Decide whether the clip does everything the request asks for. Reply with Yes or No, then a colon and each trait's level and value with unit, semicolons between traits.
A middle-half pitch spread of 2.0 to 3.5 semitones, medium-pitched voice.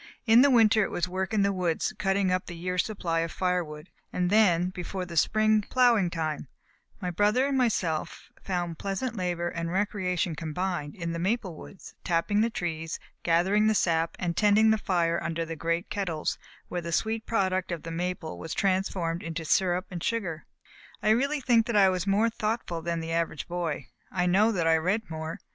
No: average, 3.9 semitones; medium, 180 Hz